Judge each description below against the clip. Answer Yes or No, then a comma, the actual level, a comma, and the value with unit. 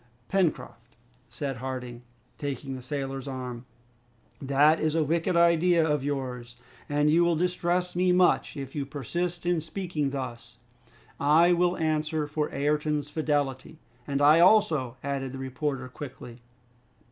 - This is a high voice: No, medium, 145 Hz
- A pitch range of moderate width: Yes, average, 3.7 semitones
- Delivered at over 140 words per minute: No, slow, 135 wpm